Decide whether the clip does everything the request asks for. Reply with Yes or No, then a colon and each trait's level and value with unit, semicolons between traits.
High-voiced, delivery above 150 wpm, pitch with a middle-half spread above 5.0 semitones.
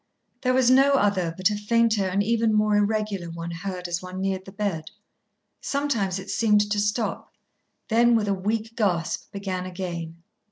No: high, 205 Hz; average, 170 wpm; average, 3.2 semitones